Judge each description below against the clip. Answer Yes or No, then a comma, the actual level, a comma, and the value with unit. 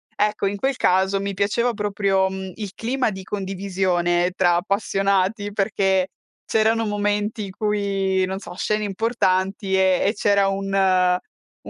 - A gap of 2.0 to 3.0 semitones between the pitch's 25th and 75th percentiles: No, narrow, 1.6 semitones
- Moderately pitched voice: No, high, 195 Hz